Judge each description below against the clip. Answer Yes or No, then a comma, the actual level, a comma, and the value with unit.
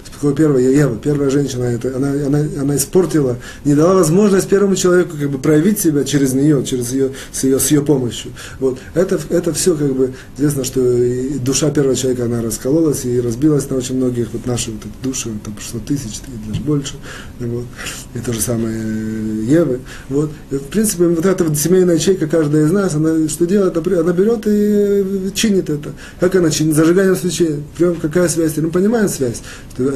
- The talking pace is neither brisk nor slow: No, fast, 185 wpm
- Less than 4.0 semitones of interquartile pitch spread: No, average, 5.1 semitones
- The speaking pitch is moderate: Yes, medium, 145 Hz